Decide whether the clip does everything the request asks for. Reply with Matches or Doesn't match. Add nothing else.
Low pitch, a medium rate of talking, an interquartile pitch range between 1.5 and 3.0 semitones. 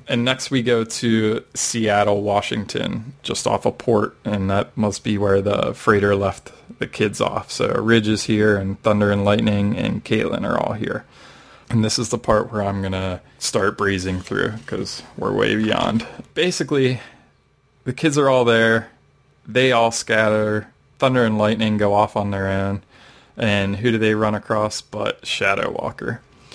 Matches